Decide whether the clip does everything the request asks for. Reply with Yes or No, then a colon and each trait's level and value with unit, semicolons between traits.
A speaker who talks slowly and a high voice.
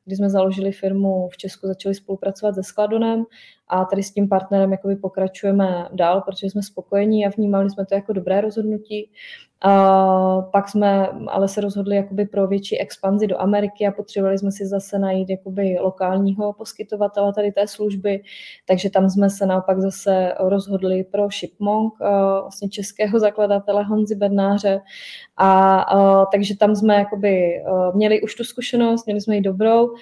No: average, 160 wpm; high, 200 Hz